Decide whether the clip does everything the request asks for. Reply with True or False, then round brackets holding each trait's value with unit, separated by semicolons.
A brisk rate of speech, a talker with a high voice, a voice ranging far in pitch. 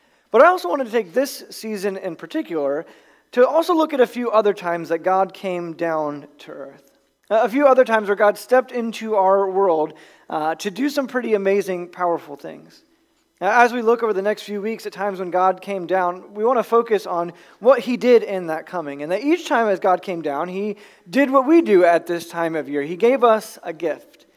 True (225 wpm; 205 Hz; 5.8 semitones)